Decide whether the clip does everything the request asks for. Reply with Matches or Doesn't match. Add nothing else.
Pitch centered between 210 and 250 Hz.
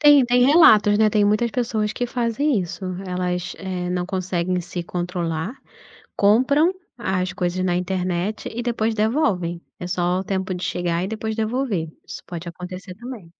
Doesn't match